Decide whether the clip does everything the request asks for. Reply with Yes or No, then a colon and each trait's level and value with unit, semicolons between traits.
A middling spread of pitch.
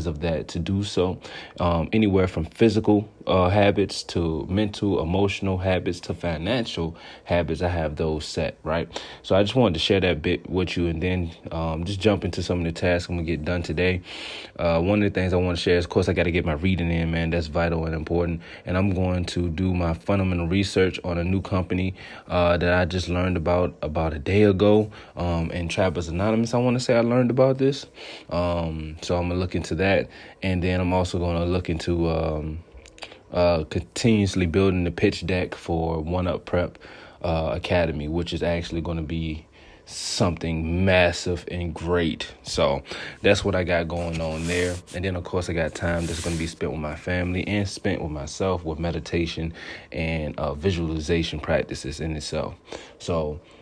No: narrow, 2.1 semitones